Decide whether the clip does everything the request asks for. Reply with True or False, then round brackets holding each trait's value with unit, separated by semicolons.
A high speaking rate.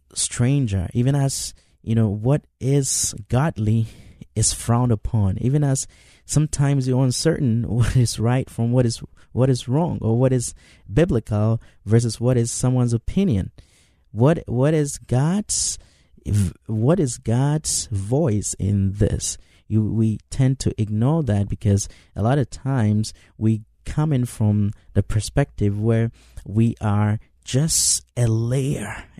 False (140 wpm)